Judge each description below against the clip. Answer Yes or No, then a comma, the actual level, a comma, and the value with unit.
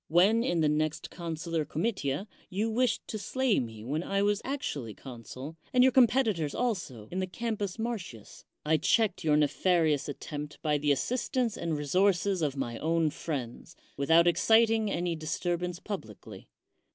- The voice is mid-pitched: Yes, medium, 170 Hz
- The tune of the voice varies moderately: No, wide, 6.2 semitones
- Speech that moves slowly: No, average, 150 wpm